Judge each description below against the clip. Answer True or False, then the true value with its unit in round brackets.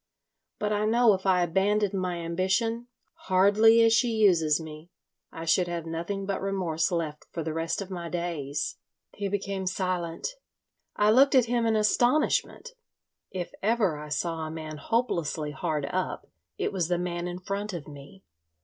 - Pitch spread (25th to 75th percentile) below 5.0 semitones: True (4.1 semitones)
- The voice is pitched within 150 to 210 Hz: True (185 Hz)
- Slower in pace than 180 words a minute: True (160 wpm)